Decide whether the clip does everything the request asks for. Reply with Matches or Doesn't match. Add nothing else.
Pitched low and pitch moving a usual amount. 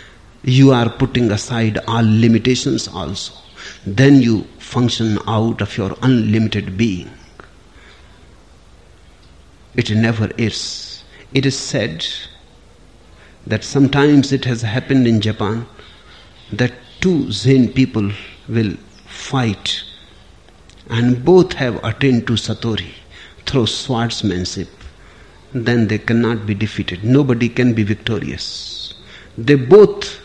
Matches